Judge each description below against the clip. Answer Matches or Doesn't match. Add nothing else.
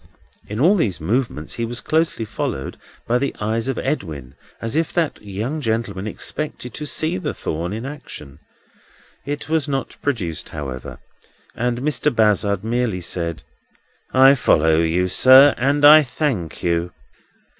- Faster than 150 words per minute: Doesn't match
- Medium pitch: Doesn't match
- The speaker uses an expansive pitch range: Matches